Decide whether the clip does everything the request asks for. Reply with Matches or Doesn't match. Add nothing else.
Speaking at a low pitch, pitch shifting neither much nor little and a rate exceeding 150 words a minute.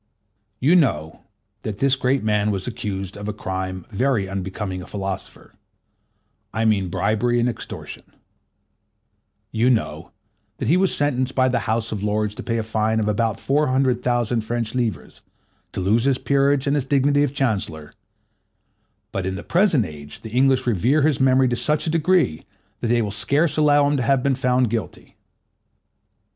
Matches